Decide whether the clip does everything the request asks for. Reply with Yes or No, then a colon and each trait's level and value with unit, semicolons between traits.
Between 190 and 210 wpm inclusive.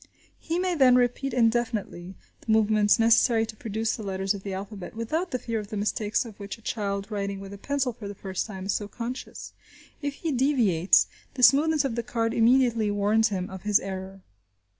Yes: fast, 205 wpm